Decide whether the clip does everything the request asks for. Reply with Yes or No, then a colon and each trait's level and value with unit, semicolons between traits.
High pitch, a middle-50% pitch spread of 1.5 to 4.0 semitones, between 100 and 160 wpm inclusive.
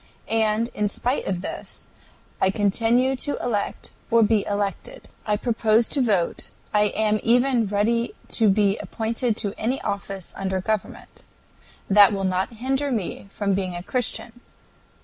Yes: high, 215 Hz; average, 2.8 semitones; average, 150 wpm